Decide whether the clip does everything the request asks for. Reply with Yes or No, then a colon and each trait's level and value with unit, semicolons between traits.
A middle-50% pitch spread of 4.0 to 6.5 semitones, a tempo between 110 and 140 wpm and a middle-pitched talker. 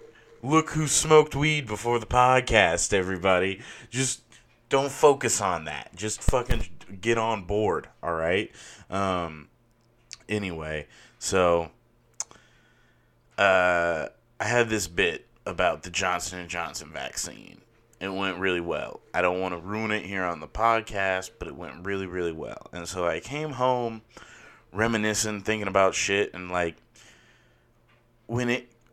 No: average, 4.6 semitones; slow, 135 wpm; low, 105 Hz